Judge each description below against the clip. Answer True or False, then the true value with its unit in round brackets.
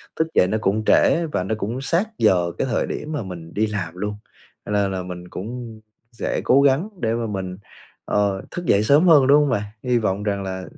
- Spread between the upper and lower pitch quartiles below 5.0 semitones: False (5.6 semitones)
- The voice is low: True (105 Hz)